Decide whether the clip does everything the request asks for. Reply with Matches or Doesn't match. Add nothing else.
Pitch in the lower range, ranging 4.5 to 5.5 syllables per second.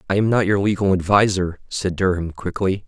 Matches